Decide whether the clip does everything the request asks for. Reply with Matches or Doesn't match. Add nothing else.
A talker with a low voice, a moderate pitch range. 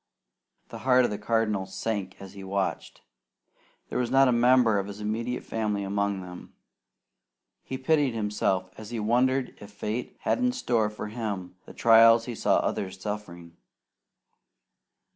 Matches